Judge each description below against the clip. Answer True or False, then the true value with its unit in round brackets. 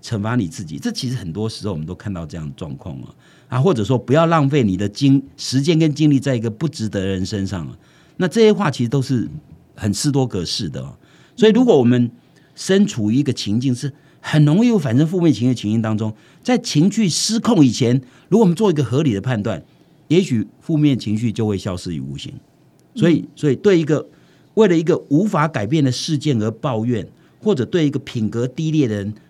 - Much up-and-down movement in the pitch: True (6.9 semitones)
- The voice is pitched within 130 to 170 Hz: True (135 Hz)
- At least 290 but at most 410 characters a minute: True (330 characters per minute)